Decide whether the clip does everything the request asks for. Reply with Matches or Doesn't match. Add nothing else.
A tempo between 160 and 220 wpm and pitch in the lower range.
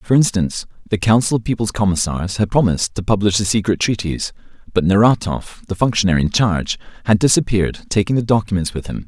Matches